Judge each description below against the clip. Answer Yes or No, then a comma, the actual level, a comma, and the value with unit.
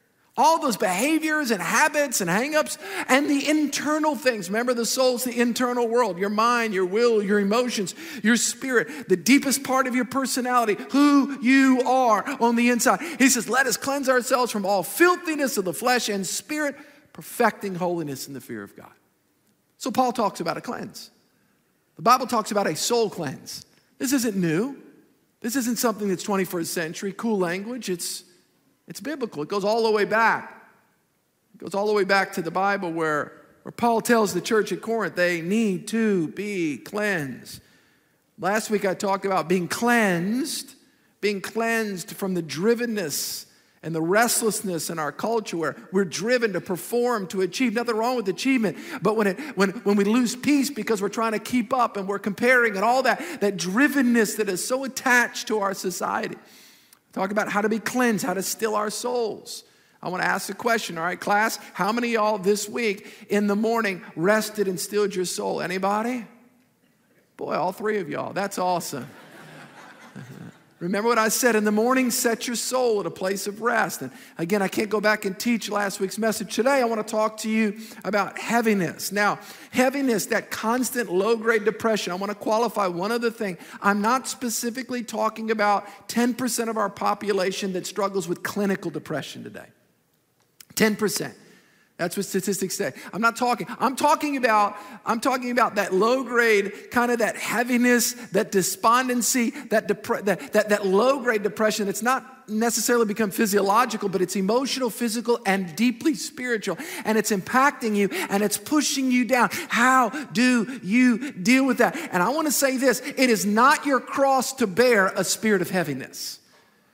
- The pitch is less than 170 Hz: No, high, 220 Hz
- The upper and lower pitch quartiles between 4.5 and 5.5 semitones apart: No, average, 3.8 semitones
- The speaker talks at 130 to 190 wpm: Yes, average, 180 wpm